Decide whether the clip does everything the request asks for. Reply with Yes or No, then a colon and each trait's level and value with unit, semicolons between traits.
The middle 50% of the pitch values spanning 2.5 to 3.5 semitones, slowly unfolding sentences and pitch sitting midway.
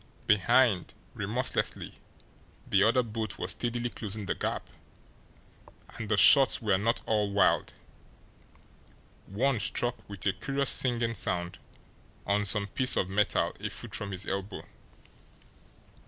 No: average, 3.2 semitones; slow, 125 wpm; low, 105 Hz